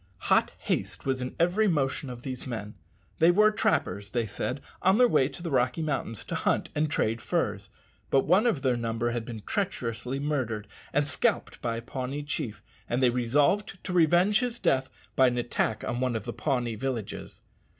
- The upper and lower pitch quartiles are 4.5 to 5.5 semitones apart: Yes, average, 5.0 semitones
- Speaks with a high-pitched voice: No, low, 130 Hz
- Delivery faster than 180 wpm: Yes, average, 190 wpm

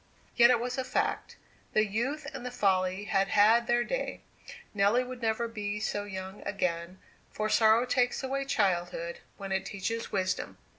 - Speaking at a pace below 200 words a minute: Yes, average, 165 wpm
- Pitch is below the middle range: No, high, 215 Hz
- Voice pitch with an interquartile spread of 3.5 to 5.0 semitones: Yes, average, 3.8 semitones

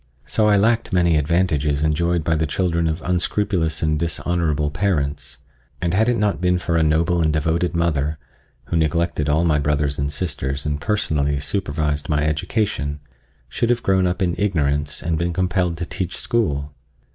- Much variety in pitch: No, average, 3.4 semitones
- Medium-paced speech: Yes, average, 170 wpm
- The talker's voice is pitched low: Yes, very low, 80 Hz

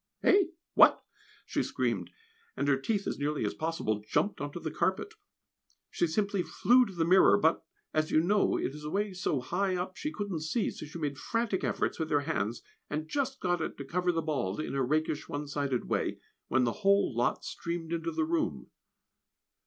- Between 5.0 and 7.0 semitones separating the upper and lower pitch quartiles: Yes, wide, 5.4 semitones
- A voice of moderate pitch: Yes, medium, 165 Hz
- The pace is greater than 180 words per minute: Yes, average, 200 wpm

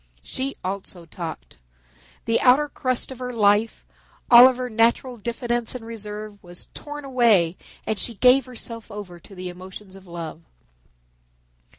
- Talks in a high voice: Yes, high, 225 Hz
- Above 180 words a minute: No, average, 150 wpm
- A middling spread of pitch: Yes, average, 4.8 semitones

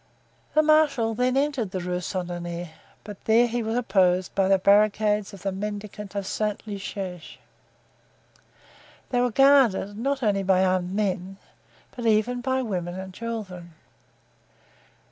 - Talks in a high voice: Yes, high, 205 Hz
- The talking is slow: No, average, 145 wpm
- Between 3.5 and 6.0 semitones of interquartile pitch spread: Yes, average, 3.8 semitones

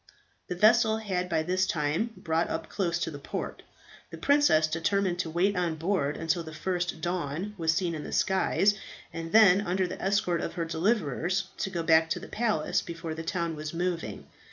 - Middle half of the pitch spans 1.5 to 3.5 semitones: Yes, average, 2.9 semitones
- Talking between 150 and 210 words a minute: Yes, average, 195 wpm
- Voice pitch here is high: No, medium, 175 Hz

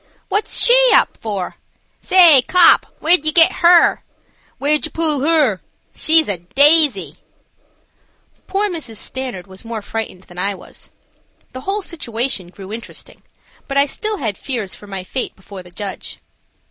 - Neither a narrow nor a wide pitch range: No, wide, 8.5 semitones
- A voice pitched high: Yes, very high, 260 Hz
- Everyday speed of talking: Yes, average, 160 wpm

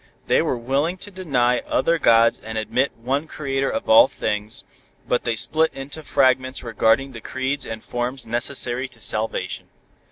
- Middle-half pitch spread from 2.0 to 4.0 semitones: Yes, average, 3.3 semitones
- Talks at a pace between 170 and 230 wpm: No, average, 160 wpm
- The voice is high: No, low, 130 Hz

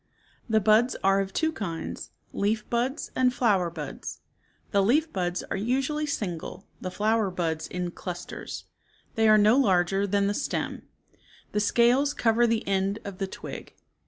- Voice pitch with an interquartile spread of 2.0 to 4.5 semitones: Yes, average, 3.9 semitones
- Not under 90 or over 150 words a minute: No, average, 165 wpm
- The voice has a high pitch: Yes, high, 205 Hz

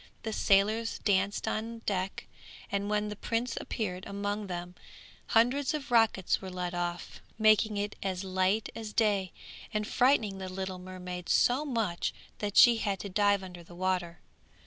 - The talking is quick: No, average, 160 wpm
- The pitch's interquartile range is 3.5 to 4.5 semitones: No, average, 3.0 semitones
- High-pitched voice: Yes, high, 200 Hz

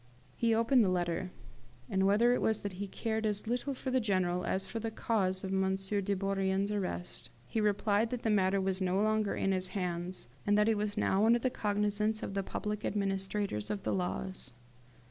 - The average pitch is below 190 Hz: No, high, 200 Hz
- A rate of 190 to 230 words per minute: Yes, fast, 205 wpm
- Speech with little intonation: Yes, narrow, 2.3 semitones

